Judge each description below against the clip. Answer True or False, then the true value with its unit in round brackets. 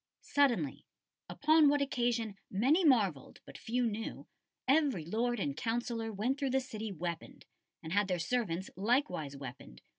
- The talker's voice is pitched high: True (225 Hz)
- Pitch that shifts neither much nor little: False (5.9 semitones)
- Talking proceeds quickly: False (145 wpm)